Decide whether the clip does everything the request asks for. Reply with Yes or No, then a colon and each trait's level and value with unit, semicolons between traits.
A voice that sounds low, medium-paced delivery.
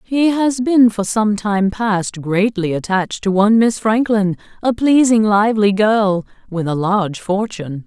No: high, 210 Hz; average, 160 wpm